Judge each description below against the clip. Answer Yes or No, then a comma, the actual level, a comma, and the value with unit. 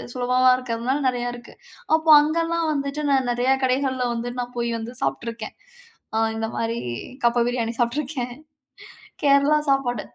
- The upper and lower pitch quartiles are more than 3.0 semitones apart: No, average, 2.7 semitones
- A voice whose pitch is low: No, very high, 250 Hz